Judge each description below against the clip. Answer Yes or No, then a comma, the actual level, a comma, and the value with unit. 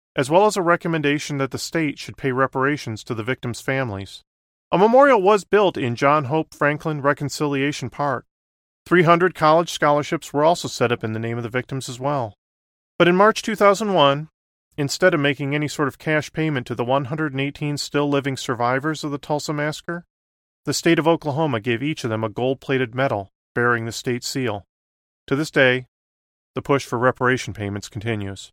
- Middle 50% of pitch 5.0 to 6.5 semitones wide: No, average, 4.4 semitones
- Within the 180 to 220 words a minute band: Yes, average, 185 wpm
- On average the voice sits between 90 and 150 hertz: Yes, medium, 140 Hz